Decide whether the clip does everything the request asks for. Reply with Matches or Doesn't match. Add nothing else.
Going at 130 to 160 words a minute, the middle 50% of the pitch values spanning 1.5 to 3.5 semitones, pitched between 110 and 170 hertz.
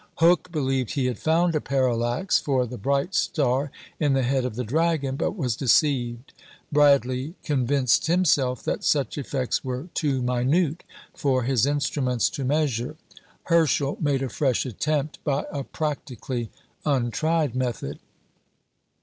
Matches